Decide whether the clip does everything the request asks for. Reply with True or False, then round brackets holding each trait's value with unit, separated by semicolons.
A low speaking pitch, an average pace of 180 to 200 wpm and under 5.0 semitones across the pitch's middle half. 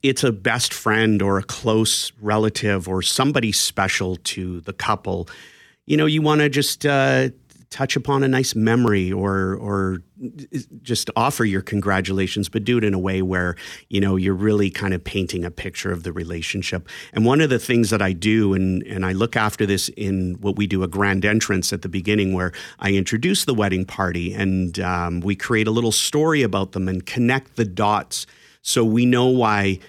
True (100 Hz; 195 wpm; 3.6 semitones)